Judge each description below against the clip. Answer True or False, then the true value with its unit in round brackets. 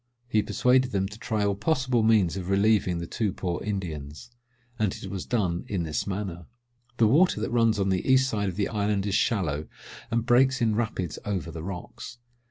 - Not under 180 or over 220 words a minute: True (195 wpm)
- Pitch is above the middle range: False (100 Hz)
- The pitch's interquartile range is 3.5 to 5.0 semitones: True (3.8 semitones)